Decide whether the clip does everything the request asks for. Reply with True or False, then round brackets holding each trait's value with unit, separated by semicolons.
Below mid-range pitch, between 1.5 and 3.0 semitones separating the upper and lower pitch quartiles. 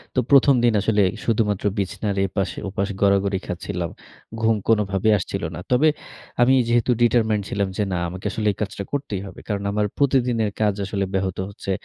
True (105 Hz; 2.6 semitones)